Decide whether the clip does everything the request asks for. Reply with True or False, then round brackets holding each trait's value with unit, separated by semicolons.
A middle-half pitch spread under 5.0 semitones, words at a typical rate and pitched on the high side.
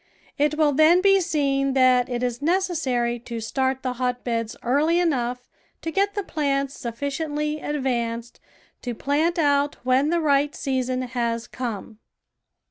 True (3.6 semitones; 145 wpm; 275 Hz)